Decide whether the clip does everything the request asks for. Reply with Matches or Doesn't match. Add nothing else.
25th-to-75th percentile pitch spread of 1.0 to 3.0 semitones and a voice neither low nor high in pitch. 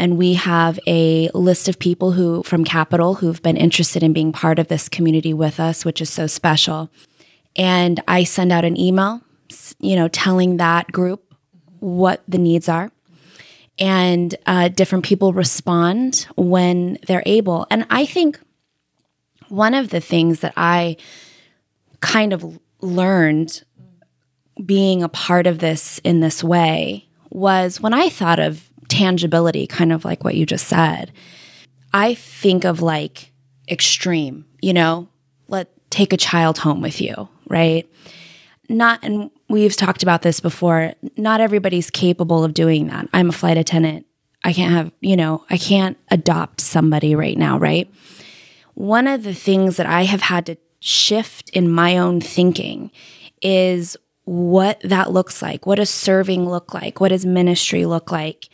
Matches